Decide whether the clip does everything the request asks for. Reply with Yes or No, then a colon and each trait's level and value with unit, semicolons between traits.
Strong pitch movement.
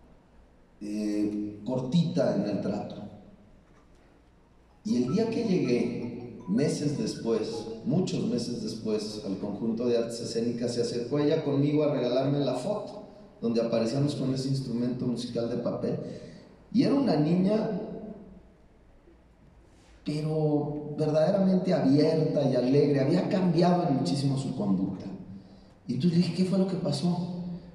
Yes: wide, 7.0 semitones